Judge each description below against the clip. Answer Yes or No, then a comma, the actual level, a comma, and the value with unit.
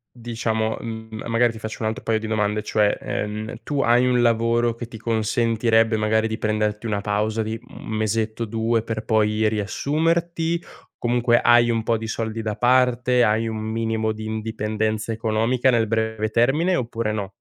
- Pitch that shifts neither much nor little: No, narrow, 1.5 semitones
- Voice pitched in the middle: No, low, 110 Hz